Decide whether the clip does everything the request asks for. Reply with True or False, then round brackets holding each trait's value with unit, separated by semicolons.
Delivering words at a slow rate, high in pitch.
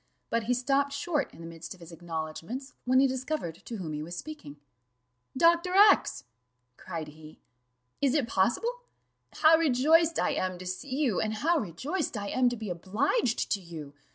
False (180 wpm; 230 Hz)